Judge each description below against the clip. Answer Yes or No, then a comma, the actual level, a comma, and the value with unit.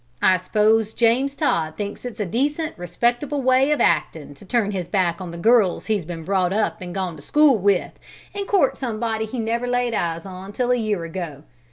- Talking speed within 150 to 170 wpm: No, fast, 205 wpm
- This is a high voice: Yes, high, 215 Hz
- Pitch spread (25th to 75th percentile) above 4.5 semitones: Yes, wide, 5.4 semitones